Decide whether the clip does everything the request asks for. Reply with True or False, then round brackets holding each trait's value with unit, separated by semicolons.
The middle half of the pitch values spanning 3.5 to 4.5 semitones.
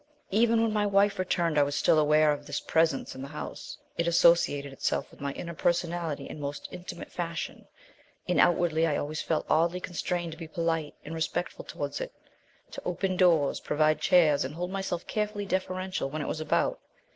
False (3.0 semitones)